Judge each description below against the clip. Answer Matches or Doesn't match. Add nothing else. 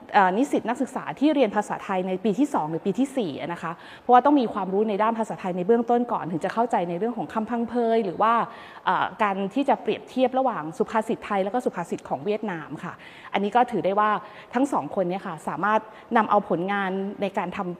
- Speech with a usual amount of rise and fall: Matches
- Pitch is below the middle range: Doesn't match